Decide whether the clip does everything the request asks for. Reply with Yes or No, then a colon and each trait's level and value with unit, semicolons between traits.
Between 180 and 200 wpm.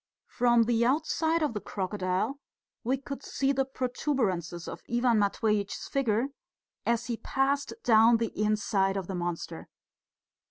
No: slow, 135 wpm